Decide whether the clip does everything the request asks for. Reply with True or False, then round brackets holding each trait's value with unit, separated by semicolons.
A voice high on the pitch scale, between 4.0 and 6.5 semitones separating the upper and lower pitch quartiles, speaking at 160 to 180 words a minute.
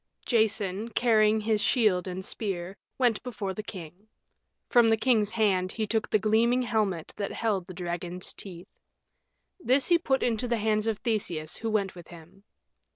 False (215 Hz; 3.4 semitones; 165 wpm)